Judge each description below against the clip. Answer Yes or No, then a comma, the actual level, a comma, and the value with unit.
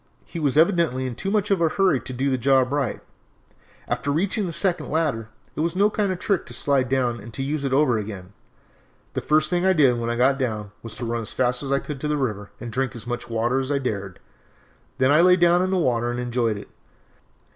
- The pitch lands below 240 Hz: Yes, low, 135 Hz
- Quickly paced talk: Yes, fast, 255 wpm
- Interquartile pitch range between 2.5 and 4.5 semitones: No, wide, 5.4 semitones